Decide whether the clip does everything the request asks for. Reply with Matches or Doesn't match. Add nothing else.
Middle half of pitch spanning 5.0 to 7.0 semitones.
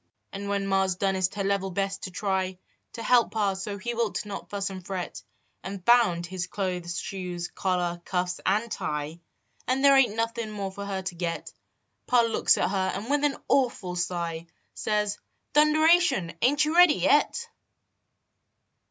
Doesn't match